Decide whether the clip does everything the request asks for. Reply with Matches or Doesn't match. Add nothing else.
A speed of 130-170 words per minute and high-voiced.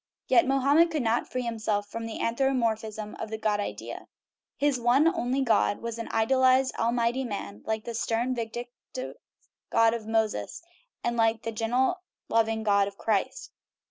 Matches